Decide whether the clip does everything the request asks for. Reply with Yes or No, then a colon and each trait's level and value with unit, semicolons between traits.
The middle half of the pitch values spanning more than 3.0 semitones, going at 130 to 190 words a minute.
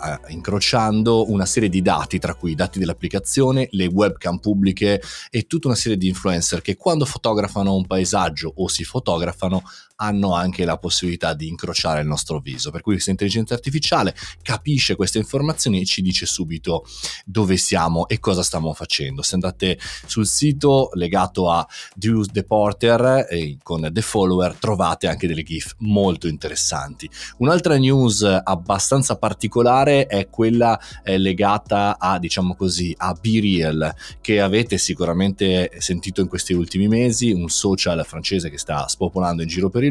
Yes: average, 3.9 semitones; average, 150 wpm